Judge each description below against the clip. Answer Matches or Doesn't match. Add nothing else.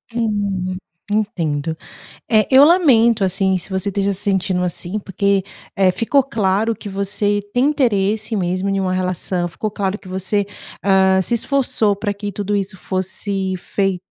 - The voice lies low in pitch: Doesn't match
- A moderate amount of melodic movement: Doesn't match